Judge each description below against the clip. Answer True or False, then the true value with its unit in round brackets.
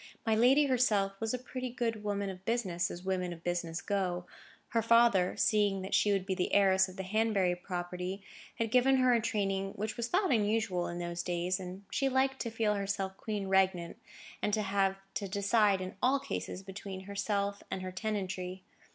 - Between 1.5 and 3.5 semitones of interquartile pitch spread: True (3.1 semitones)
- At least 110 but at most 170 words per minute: False (195 wpm)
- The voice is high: True (200 Hz)